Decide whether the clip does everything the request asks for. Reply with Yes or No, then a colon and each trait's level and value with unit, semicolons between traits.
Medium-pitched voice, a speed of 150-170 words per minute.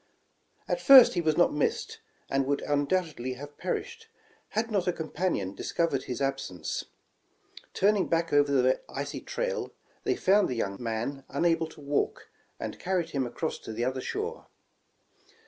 Yes: medium, 150 Hz; average, 160 wpm